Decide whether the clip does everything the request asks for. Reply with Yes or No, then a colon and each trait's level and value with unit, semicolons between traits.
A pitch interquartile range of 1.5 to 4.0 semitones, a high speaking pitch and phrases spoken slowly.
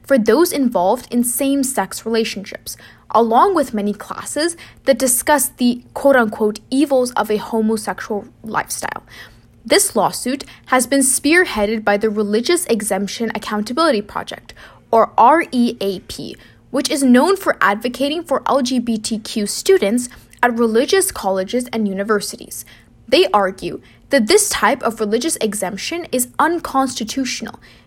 No: average, 4.6 semitones; high, 235 Hz; slow, 125 wpm